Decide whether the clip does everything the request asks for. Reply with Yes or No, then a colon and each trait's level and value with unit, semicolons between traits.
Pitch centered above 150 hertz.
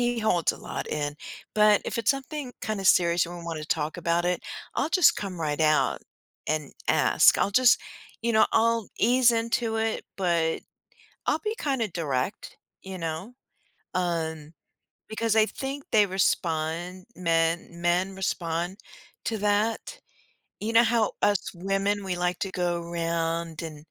Yes: medium, 185 Hz